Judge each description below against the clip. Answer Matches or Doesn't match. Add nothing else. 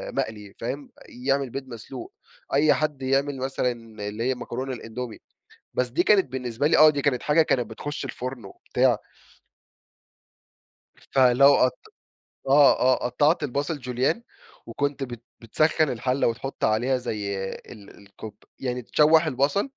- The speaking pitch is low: Matches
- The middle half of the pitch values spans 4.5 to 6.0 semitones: Doesn't match